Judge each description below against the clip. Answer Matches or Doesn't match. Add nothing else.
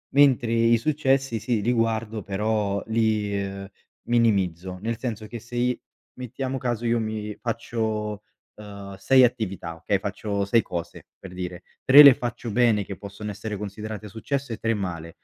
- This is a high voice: Doesn't match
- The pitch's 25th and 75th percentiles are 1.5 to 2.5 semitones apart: Doesn't match